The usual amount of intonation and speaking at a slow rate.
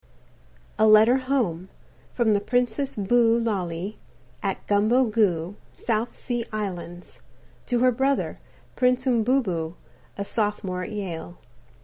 Yes: average, 4.4 semitones; slow, 120 wpm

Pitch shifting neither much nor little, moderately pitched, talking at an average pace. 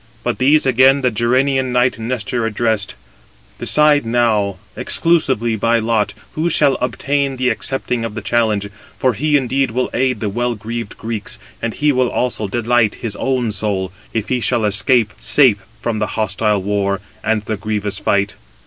No: average, 3.3 semitones; low, 115 Hz; average, 165 wpm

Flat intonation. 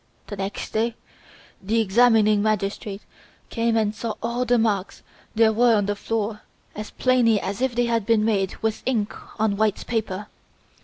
Yes: narrow, 2.0 semitones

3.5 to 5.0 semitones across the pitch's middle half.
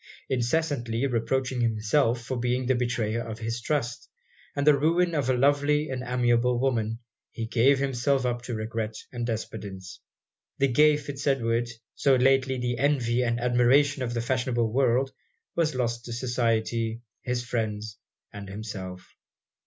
No: narrow, 2.6 semitones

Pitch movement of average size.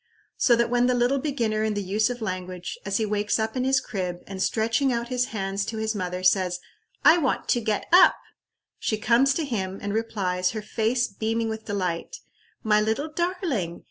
Yes: average, 3.8 semitones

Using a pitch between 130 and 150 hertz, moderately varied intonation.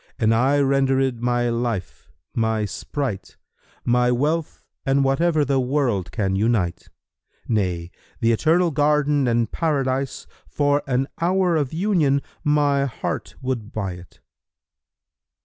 Yes: low, 135 Hz; average, 4.1 semitones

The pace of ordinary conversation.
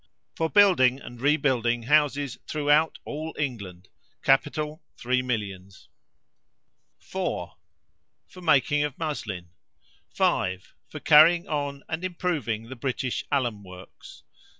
No: slow, 105 wpm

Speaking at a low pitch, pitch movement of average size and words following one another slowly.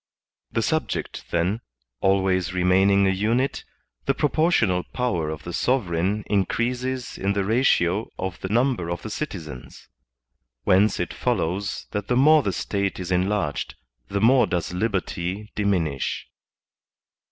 Yes: low, 100 Hz; average, 4.3 semitones; slow, 130 wpm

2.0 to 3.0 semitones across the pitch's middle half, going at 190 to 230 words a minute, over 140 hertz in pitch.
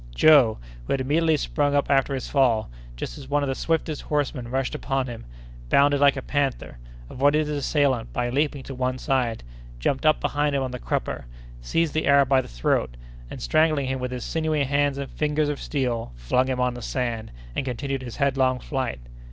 No: narrow, 2.4 semitones; average, 200 wpm; low, 135 Hz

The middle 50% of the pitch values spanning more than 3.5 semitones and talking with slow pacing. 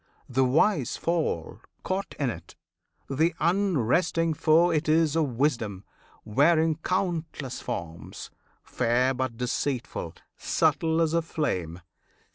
Yes: average, 5.1 semitones; slow, 110 wpm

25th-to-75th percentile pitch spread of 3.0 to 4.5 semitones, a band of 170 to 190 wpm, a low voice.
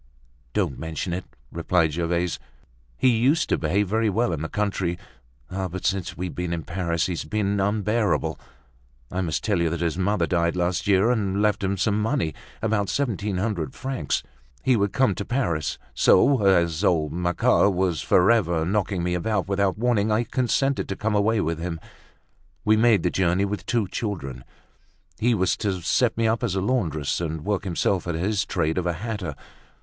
Yes: average, 3.8 semitones; average, 180 wpm; very low, 95 Hz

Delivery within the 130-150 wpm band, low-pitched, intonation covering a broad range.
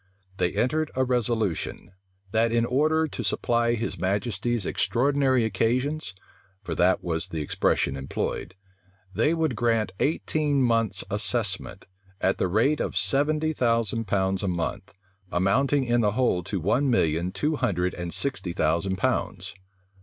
Yes: average, 140 wpm; low, 115 Hz; wide, 5.7 semitones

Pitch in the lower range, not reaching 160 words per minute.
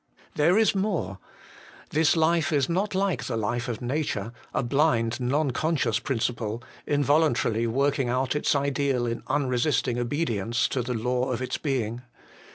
Yes: low, 130 Hz; average, 150 wpm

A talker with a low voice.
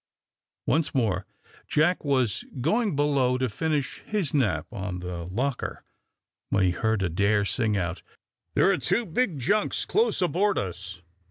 Yes: low, 125 Hz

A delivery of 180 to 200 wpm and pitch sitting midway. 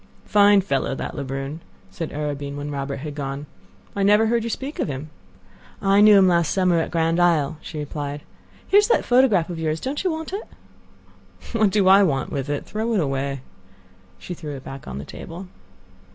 Yes: average, 195 wpm; medium, 165 Hz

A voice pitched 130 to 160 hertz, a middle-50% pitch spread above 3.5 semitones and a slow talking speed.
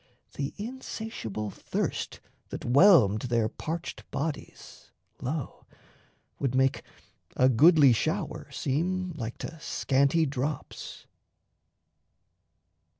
Yes: medium, 140 Hz; average, 4.7 semitones; slow, 90 wpm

